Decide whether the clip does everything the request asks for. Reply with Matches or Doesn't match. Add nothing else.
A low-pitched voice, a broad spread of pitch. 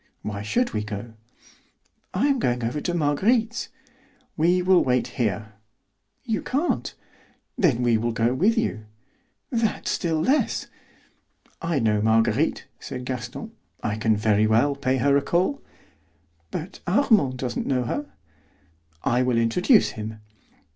Matches